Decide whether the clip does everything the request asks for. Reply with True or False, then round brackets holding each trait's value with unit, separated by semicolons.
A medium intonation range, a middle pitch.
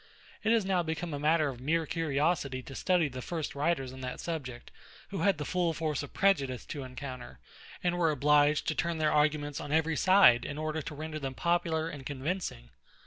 True (3.2 semitones; 155 Hz)